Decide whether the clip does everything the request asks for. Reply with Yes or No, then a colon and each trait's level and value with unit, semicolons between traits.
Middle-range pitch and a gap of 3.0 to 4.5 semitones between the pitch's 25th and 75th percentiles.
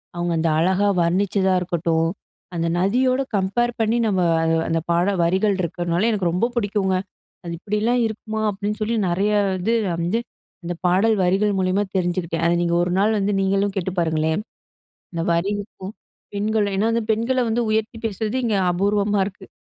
No: high, 195 Hz; average, 3.6 semitones